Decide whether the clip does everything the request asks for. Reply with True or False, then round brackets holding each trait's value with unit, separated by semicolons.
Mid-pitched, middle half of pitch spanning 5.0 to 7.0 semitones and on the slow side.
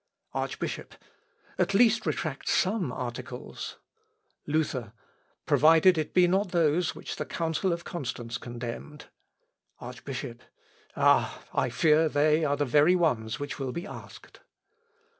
True (150 Hz; 5.4 semitones; 120 wpm)